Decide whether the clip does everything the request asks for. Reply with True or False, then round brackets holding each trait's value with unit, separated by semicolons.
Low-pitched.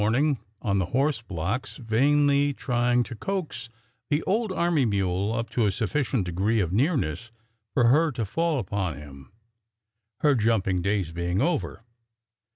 True (115 Hz)